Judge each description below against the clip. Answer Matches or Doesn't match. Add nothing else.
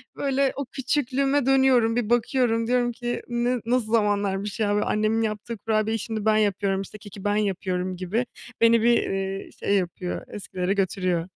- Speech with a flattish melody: Doesn't match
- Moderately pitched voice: Doesn't match